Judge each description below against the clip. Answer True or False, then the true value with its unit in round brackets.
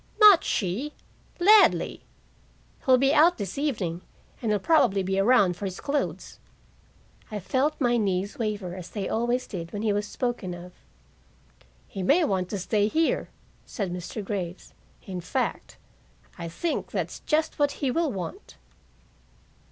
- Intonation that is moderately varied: False (6.9 semitones)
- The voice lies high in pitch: True (210 Hz)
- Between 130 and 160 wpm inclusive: True (150 wpm)